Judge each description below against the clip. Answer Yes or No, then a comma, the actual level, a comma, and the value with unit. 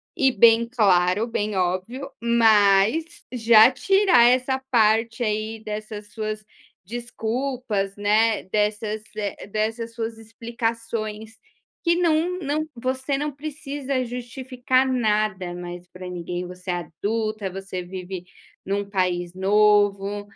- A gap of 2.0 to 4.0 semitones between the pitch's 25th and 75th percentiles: Yes, average, 3.7 semitones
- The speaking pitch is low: No, high, 220 Hz